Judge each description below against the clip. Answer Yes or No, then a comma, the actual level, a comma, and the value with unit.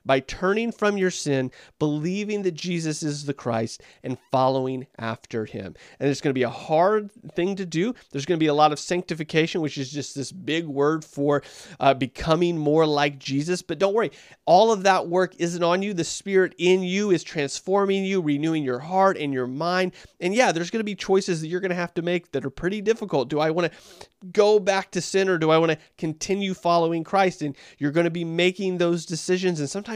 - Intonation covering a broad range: No, average, 4.3 semitones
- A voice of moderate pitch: Yes, medium, 170 Hz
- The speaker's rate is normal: No, fast, 225 wpm